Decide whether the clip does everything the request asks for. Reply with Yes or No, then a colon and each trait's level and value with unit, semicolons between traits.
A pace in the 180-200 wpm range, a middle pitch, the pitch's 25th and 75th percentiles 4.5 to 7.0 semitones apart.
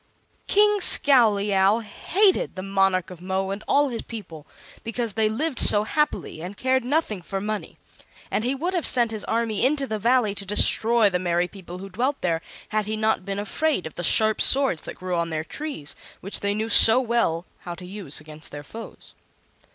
No: average, 195 wpm; high, 210 Hz; average, 4.8 semitones